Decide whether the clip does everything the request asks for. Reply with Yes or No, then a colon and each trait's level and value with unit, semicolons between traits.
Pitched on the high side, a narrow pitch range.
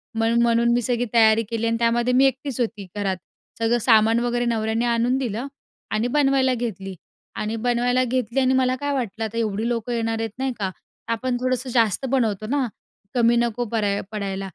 Yes: high, 235 Hz; narrow, 2.1 semitones